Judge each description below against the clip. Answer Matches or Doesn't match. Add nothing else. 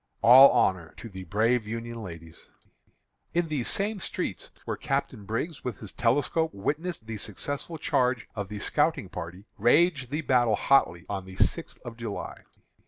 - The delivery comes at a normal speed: Matches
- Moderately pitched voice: Doesn't match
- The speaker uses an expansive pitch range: Matches